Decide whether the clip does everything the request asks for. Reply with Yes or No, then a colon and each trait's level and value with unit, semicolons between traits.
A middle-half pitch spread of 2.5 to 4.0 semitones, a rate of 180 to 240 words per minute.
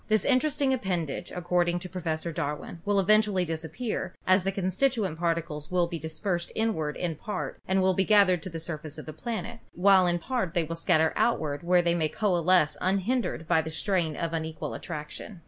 Yes: average, 3.6 semitones; average, 190 wpm